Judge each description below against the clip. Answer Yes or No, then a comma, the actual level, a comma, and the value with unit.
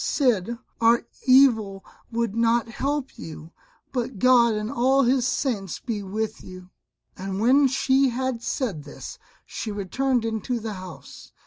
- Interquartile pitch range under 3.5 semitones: No, average, 4.2 semitones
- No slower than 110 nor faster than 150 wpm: Yes, average, 140 wpm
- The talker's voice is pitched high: Yes, high, 230 Hz